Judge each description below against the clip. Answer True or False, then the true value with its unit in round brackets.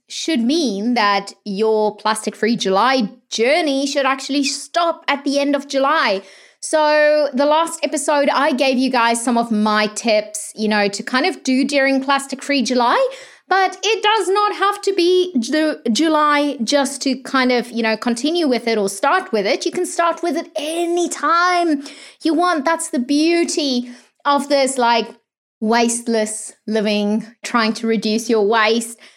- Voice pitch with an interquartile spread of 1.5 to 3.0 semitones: False (5.4 semitones)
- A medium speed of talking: True (170 wpm)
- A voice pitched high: True (275 Hz)